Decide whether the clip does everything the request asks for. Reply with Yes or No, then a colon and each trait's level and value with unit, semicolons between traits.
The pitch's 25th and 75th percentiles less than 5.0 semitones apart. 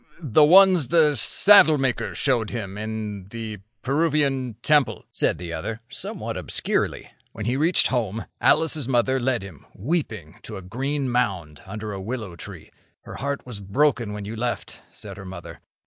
No: wide, 5.5 semitones